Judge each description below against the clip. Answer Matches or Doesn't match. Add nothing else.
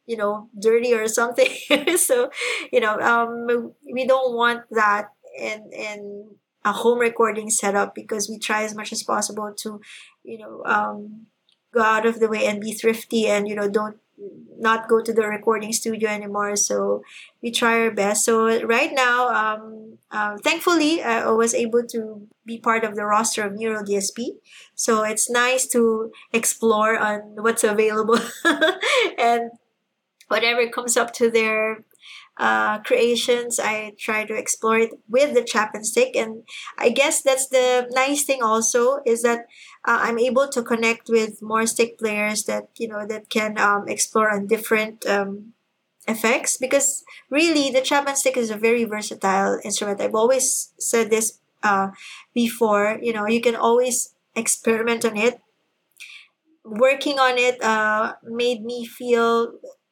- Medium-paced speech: Matches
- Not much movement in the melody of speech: Matches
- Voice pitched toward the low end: Doesn't match